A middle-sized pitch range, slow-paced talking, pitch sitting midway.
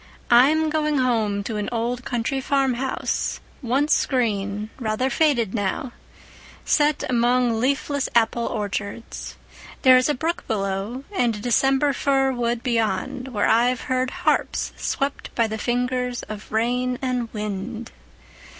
No: average, 3.1 semitones; slow, 130 wpm; high, 245 Hz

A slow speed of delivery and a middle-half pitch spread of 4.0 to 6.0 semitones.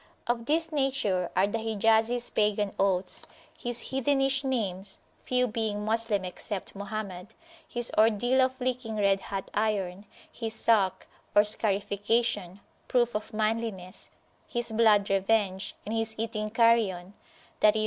No: slow, 120 wpm; average, 2.8 semitones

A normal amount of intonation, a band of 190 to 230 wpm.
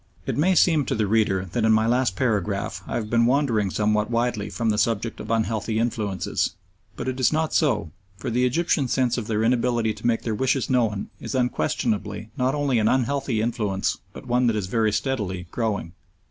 Yes: average, 3.1 semitones; average, 200 wpm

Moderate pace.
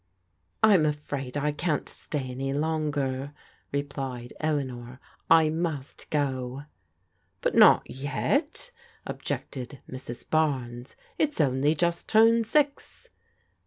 No: slow, 120 wpm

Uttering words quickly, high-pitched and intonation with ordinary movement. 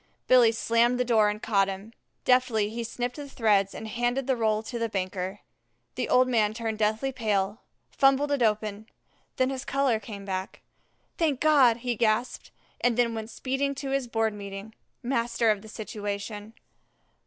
No: average, 170 wpm; high, 225 Hz; average, 3.1 semitones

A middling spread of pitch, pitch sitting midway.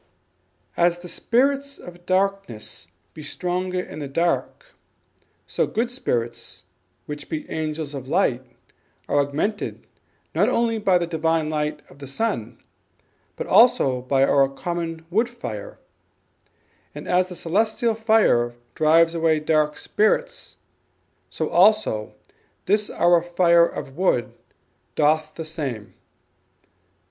Yes: average, 5.0 semitones; medium, 165 Hz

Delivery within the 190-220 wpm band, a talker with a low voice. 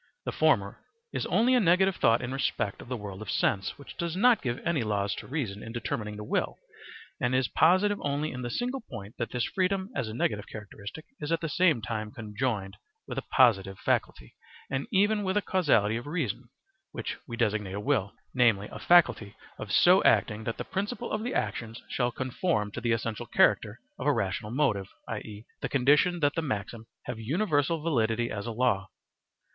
Yes: average, 195 wpm; low, 125 Hz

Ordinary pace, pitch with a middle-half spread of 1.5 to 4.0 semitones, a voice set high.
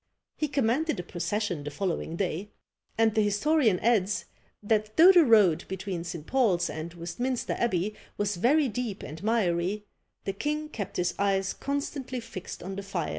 No: average, 165 wpm; wide, 5.4 semitones; high, 205 Hz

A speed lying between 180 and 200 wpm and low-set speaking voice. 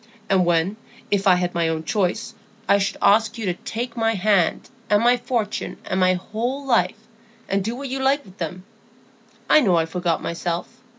No: average, 190 wpm; high, 200 Hz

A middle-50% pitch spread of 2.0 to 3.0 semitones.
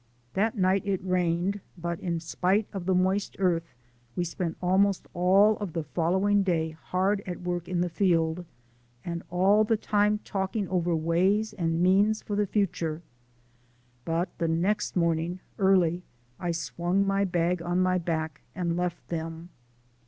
Yes: narrow, 2.6 semitones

